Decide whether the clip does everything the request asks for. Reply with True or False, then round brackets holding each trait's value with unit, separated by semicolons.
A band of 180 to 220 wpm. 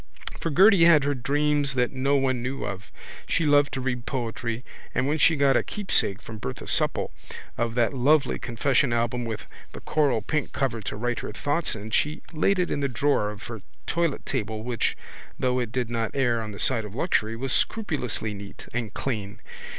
True (190 wpm)